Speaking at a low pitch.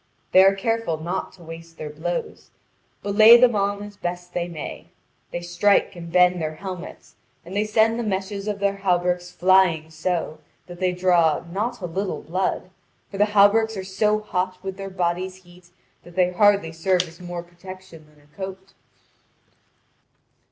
No: medium, 185 Hz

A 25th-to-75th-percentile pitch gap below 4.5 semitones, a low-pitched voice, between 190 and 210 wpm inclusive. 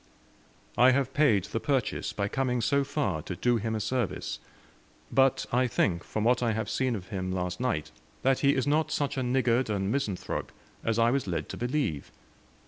No: average, 4.8 semitones; low, 120 Hz; average, 195 wpm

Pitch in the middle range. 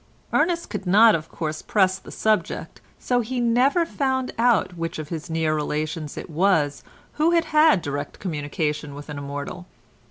Yes: medium, 180 Hz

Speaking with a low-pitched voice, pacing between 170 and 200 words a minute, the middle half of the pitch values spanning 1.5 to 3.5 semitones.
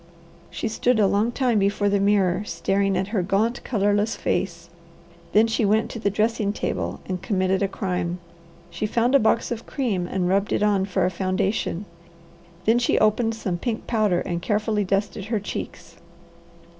No: high, 205 Hz; average, 175 wpm; average, 2.7 semitones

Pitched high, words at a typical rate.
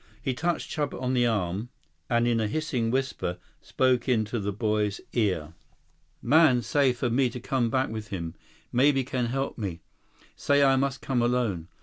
No: low, 120 Hz; average, 175 wpm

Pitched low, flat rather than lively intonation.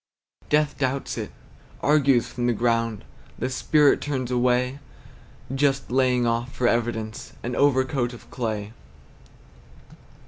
Yes: low, 125 Hz; narrow, 2.3 semitones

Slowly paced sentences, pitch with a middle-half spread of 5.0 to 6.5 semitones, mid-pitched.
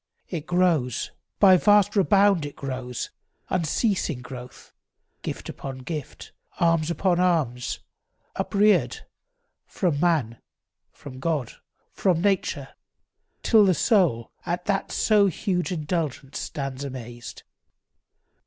Yes: slow, 105 wpm; wide, 5.6 semitones; medium, 165 Hz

